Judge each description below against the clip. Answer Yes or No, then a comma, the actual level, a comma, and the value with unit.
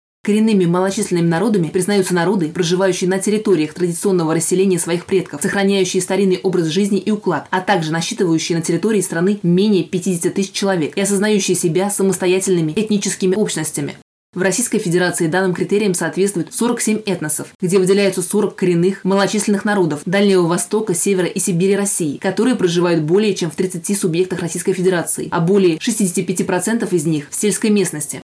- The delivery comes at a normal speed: Yes, average, 150 wpm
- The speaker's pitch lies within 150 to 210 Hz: Yes, high, 190 Hz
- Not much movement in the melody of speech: Yes, narrow, 2.2 semitones